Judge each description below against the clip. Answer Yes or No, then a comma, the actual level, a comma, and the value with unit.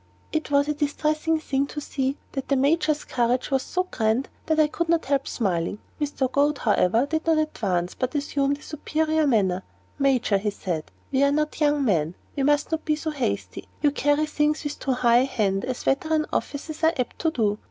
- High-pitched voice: Yes, very high, 280 Hz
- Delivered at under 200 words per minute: No, fast, 205 wpm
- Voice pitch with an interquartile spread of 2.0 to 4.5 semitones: Yes, average, 3.8 semitones